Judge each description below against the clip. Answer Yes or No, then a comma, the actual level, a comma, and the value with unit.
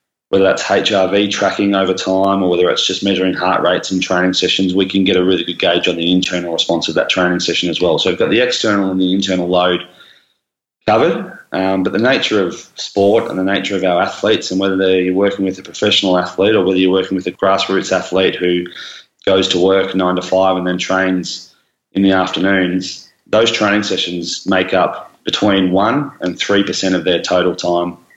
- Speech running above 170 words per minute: Yes, fast, 205 wpm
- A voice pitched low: Yes, very low, 95 Hz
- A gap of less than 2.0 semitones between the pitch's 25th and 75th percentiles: Yes, narrow, 1.1 semitones